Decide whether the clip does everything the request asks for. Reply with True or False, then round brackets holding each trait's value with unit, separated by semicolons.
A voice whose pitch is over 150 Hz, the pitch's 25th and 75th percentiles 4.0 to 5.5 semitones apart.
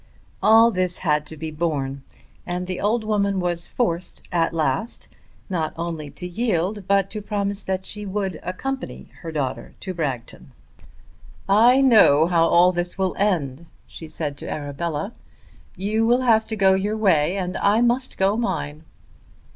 True (185 Hz; 4.4 semitones)